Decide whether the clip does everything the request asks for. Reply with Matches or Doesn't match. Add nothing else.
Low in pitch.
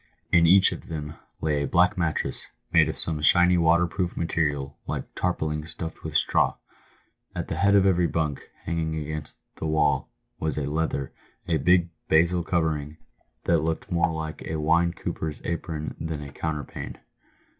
Matches